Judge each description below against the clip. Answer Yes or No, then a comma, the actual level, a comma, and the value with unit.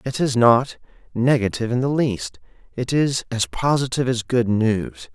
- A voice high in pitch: No, low, 120 Hz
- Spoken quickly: No, average, 165 wpm